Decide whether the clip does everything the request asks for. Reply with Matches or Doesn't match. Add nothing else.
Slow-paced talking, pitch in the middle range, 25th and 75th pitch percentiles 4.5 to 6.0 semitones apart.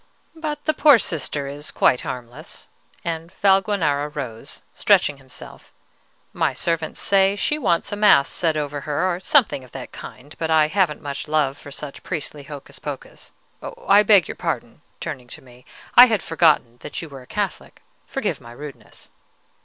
Doesn't match